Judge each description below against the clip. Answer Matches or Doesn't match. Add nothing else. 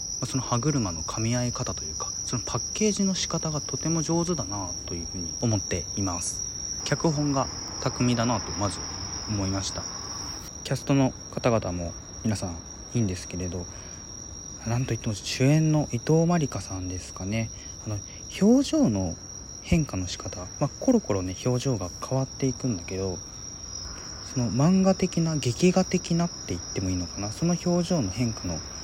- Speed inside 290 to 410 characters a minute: Matches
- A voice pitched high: Doesn't match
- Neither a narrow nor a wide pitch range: Doesn't match